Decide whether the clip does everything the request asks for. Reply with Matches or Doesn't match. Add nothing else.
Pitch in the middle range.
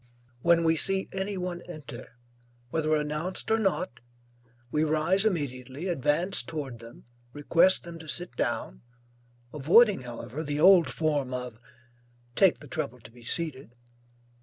Matches